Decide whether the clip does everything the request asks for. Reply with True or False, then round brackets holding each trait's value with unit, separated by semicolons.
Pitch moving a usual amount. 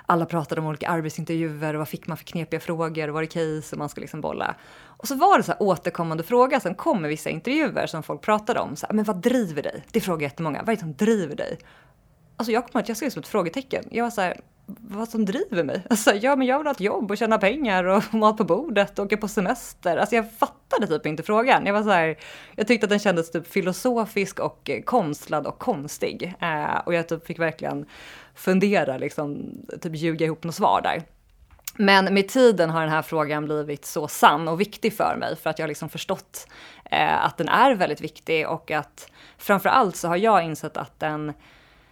False (5.7 semitones)